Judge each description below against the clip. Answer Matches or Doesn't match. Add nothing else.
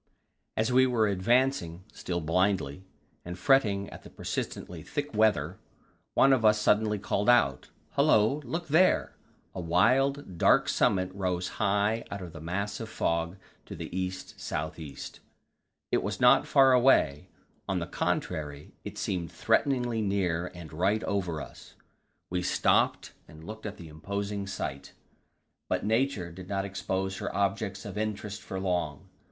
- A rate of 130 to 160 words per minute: Matches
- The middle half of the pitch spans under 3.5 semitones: Doesn't match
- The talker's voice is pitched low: Matches